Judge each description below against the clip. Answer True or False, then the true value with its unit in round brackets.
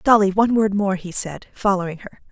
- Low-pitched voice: False (195 Hz)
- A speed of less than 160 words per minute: False (205 wpm)